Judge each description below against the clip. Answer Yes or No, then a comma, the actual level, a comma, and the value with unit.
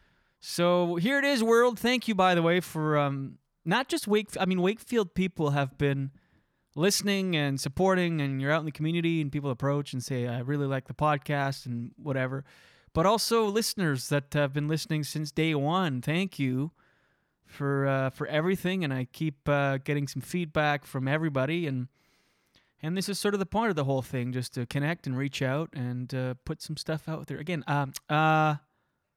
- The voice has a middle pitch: Yes, medium, 150 Hz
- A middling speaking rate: Yes, average, 190 wpm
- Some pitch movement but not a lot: Yes, average, 4.3 semitones